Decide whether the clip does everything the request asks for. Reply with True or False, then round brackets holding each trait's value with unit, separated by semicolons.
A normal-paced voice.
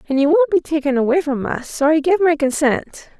False (245 wpm)